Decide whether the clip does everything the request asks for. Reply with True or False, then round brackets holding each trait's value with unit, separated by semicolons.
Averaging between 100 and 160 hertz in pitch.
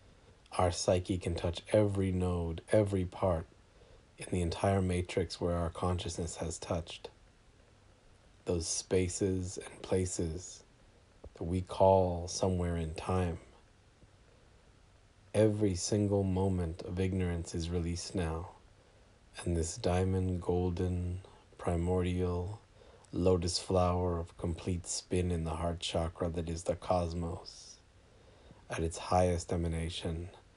False (90 Hz)